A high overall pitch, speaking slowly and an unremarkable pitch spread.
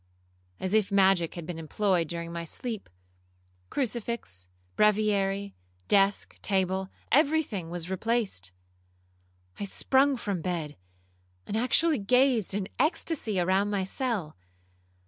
Yes: high, 200 Hz; slow, 115 wpm; average, 4.7 semitones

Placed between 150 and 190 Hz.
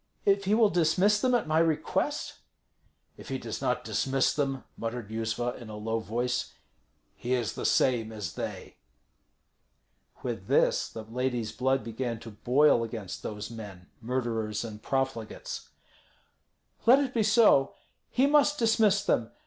No: low, 125 Hz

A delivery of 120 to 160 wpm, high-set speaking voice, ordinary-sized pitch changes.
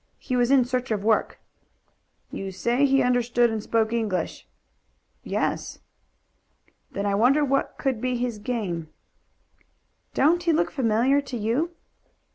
Yes: slow, 135 wpm; high, 245 Hz; average, 3.6 semitones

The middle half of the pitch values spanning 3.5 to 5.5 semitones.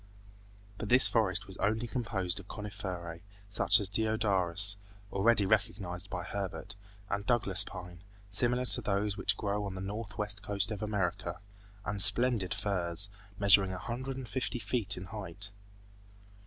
No: narrow, 2.4 semitones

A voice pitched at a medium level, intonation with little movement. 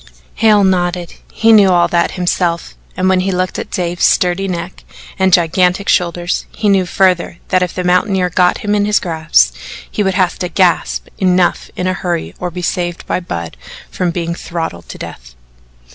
Yes: medium, 180 Hz; narrow, 1.5 semitones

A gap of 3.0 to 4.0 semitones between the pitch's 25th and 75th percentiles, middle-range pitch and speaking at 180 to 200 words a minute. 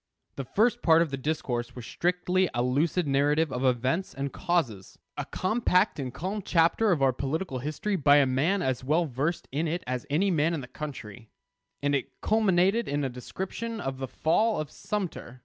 No: wide, 5.4 semitones; medium, 150 Hz; average, 190 wpm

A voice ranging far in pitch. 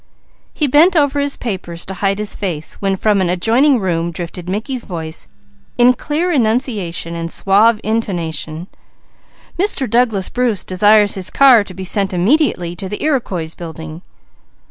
Yes: wide, 6.0 semitones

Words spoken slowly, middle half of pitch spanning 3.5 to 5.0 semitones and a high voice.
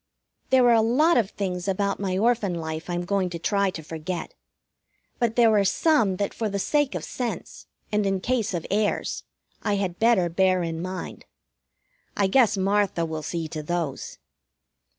No: average, 175 wpm; average, 4.0 semitones; high, 195 Hz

